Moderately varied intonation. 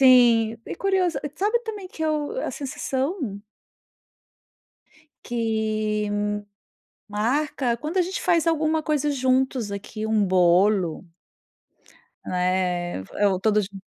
No: wide, 6.9 semitones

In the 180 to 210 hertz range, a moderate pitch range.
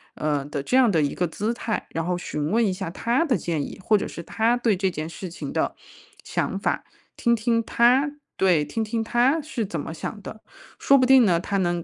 No: high, 205 Hz; wide, 5.8 semitones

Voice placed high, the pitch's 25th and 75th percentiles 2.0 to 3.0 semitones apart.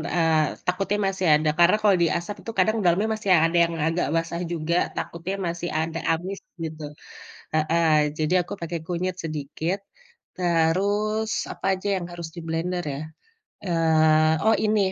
No: medium, 170 Hz; average, 2.7 semitones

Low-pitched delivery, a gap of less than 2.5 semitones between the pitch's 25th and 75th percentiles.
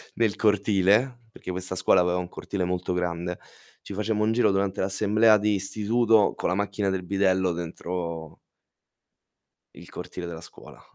No: very low, 95 Hz; average, 2.8 semitones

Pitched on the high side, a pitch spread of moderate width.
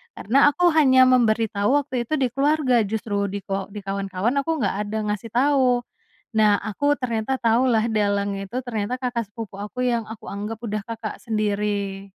Yes: high, 225 Hz; average, 3.8 semitones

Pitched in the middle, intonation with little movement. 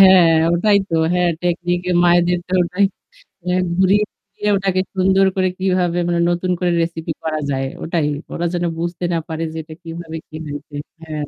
Yes: medium, 175 Hz; narrow, 2.1 semitones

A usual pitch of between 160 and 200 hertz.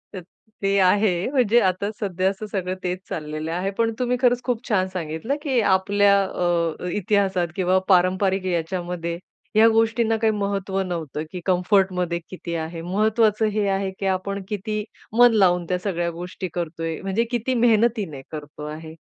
Yes: high, 190 Hz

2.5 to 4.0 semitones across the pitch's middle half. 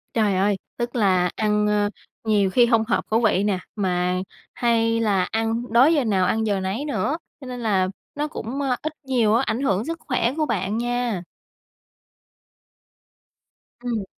Yes: average, 3.4 semitones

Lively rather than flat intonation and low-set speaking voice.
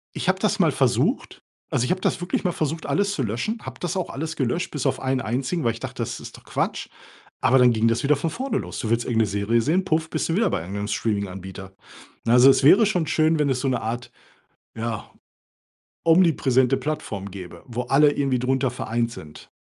Yes: wide, 5.8 semitones; low, 130 Hz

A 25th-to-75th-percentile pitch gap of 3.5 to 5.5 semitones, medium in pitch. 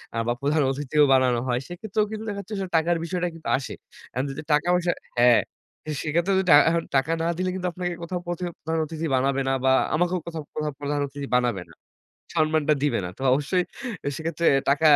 Yes: average, 4.1 semitones; medium, 160 Hz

